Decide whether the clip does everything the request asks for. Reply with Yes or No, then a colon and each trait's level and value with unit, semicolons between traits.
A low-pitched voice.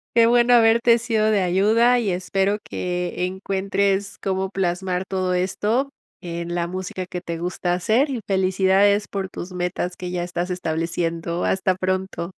No: high, 190 Hz